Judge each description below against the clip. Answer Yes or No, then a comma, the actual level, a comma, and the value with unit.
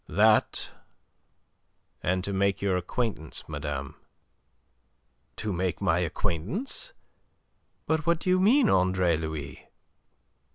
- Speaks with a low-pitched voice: Yes, very low, 95 Hz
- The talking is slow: Yes, slow, 100 wpm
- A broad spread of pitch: Yes, wide, 7.3 semitones